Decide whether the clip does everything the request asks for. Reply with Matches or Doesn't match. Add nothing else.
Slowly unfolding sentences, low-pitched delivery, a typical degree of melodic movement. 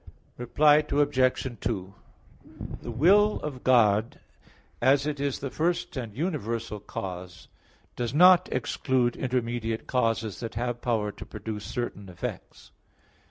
Matches